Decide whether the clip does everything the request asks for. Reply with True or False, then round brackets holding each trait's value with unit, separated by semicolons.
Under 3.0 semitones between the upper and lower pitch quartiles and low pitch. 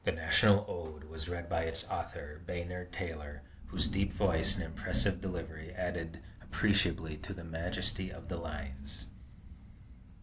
True (2.6 semitones; 85 Hz)